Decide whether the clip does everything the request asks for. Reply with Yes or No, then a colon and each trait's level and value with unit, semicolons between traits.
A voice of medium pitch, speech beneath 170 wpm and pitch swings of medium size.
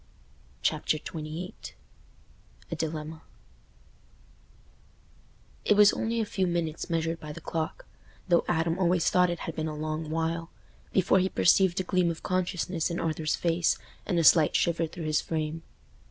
No: medium, 165 Hz; average, 145 wpm; narrow, 2.2 semitones